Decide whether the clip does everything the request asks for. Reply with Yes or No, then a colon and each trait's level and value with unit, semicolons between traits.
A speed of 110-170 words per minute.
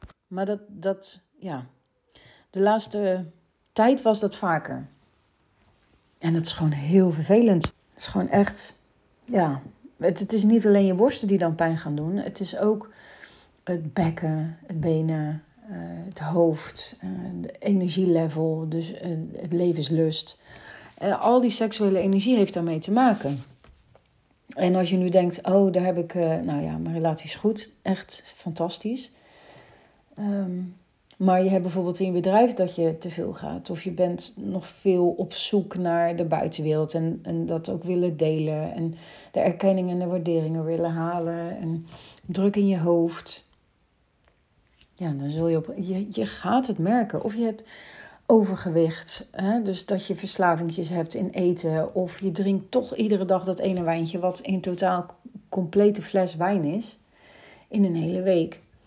Yes: average, 160 wpm